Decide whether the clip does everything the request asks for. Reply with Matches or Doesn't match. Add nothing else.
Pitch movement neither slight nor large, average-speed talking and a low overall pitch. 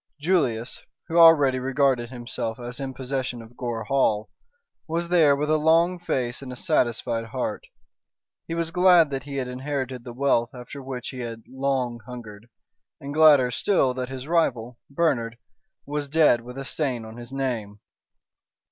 Matches